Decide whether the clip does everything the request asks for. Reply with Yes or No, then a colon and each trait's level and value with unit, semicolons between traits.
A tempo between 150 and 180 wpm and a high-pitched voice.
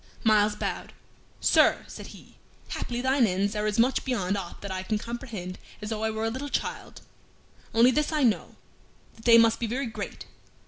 No: average, 190 wpm; high, 225 Hz